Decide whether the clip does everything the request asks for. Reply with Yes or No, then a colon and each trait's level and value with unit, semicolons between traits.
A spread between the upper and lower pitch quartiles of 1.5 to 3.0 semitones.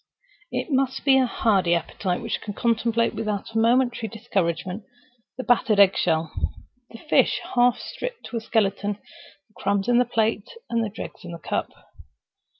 No: average, 3.6 semitones